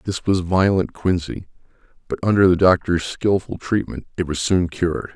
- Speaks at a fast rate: No, average, 165 wpm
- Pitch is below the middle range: Yes, very low, 90 Hz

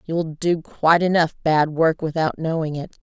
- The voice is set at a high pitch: No, medium, 160 Hz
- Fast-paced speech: No, average, 175 wpm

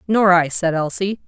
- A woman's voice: Yes, female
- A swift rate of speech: No, average, 190 wpm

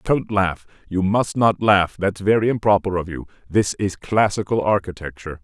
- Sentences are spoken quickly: No, average, 165 wpm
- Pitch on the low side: Yes, low, 100 Hz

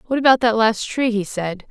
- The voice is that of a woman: Yes, female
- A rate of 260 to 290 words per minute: No, fast, 245 wpm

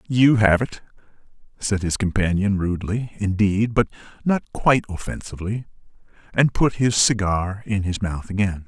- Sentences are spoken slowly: Yes, slow, 130 wpm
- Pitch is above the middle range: No, low, 105 Hz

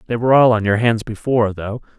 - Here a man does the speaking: Yes, male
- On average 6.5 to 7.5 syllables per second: Yes, 6.6 syllables/s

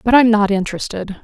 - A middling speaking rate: Yes, average, 195 wpm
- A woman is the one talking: Yes, female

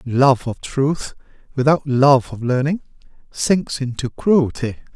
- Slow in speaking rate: Yes, slow, 120 wpm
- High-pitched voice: No, low, 135 Hz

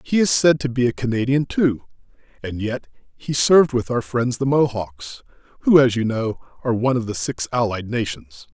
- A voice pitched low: Yes, low, 120 Hz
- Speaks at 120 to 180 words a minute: No, average, 195 wpm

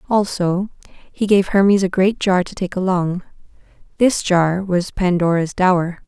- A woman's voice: Yes, female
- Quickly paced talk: No, average, 150 wpm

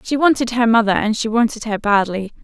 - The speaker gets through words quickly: Yes, fast, 220 wpm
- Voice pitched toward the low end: No, high, 225 Hz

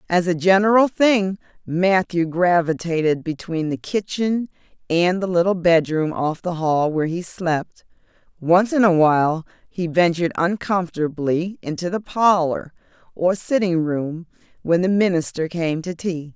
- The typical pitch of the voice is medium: Yes, medium, 175 Hz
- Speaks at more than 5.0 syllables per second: No, 4.4 syllables/s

